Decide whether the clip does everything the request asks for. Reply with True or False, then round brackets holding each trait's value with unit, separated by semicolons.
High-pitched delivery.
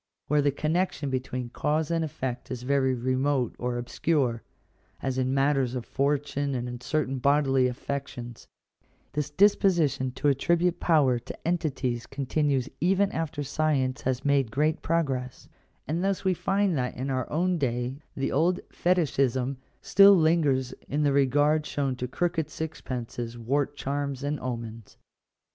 False (140 Hz)